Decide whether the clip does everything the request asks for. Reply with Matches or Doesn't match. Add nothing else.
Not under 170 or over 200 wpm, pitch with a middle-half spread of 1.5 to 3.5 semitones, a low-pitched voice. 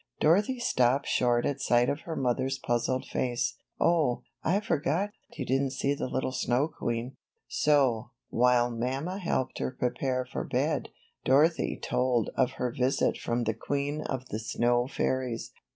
Doesn't match